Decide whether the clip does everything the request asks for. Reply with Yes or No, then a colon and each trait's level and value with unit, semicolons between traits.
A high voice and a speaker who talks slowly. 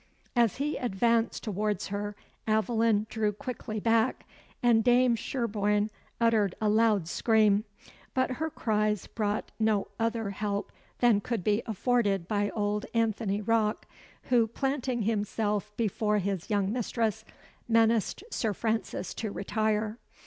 Yes: high, 220 Hz; slow, 125 wpm